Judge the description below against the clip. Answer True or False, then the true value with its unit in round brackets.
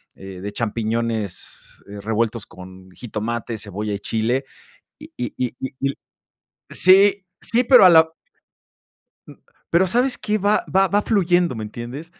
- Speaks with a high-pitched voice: False (120 Hz)